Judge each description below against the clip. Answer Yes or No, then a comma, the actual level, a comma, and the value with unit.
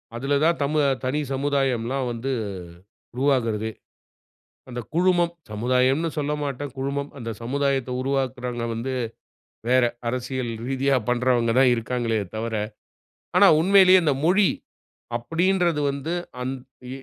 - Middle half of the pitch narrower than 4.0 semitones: Yes, average, 3.0 semitones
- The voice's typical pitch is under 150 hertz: Yes, low, 135 Hz